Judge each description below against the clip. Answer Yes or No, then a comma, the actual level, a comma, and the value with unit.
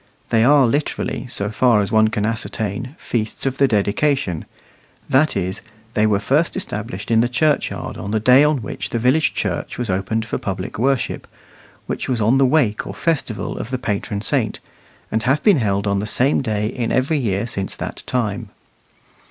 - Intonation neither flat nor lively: Yes, average, 4.3 semitones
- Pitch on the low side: Yes, low, 115 Hz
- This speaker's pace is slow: No, average, 185 wpm